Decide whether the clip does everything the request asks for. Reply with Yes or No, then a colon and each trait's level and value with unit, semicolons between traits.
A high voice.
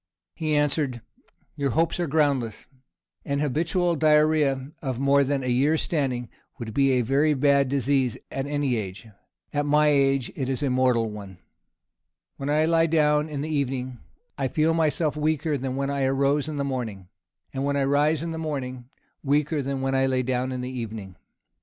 No: medium, 140 Hz